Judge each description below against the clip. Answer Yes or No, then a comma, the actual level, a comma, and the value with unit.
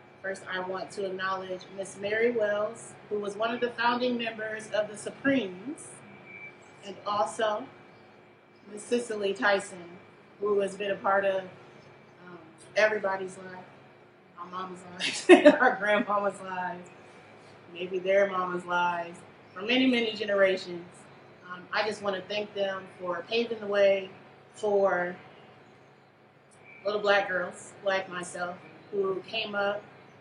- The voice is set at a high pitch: Yes, high, 195 Hz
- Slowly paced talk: Yes, slow, 130 wpm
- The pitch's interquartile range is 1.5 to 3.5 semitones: Yes, narrow, 2.5 semitones